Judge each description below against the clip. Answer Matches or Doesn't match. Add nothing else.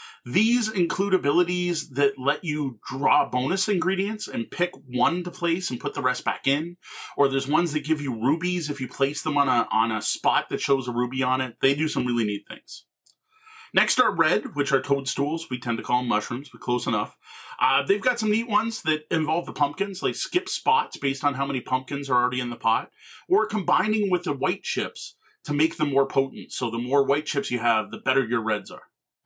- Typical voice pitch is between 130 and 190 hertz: Matches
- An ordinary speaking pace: Doesn't match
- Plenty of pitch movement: Matches